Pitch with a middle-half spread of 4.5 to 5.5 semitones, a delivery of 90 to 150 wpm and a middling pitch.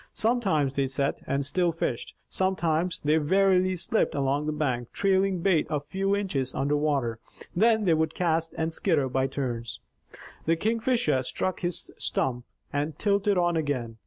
No: average, 5.2 semitones; average, 160 wpm; medium, 160 Hz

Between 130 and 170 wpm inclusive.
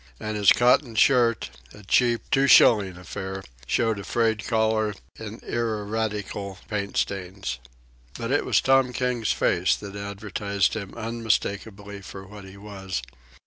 Yes: average, 140 wpm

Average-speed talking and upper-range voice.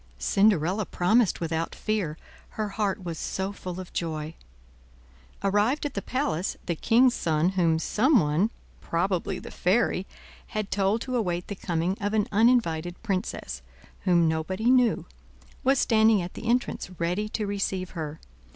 Yes: average, 150 wpm; high, 195 Hz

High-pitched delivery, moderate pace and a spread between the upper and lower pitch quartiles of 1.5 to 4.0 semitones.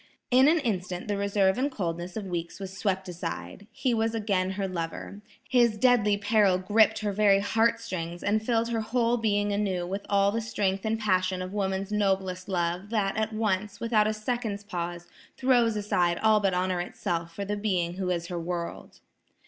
Yes: high, 200 Hz; average, 190 wpm; average, 2.9 semitones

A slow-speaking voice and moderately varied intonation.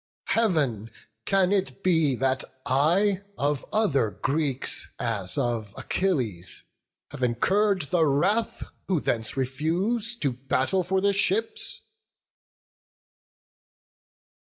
No: slow, 100 wpm; wide, 7.0 semitones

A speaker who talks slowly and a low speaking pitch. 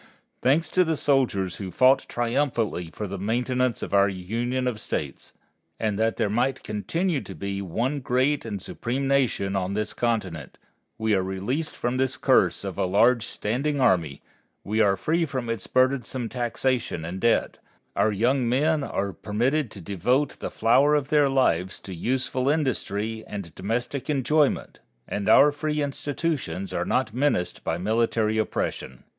No: average, 160 wpm; low, 120 Hz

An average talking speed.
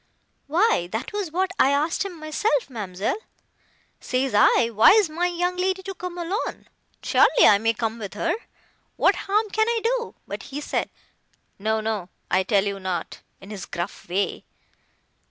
Yes: average, 155 wpm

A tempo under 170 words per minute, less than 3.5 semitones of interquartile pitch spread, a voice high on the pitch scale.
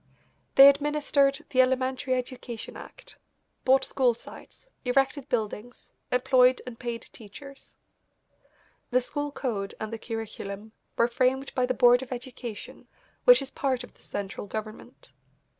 Yes: slow, 135 wpm; narrow, 2.6 semitones; very high, 250 Hz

